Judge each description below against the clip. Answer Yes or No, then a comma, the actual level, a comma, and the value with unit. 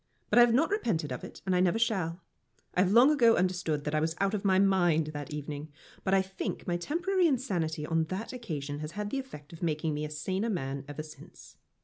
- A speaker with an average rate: No, fast, 235 wpm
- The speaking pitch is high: No, medium, 180 Hz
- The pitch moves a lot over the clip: Yes, wide, 6.2 semitones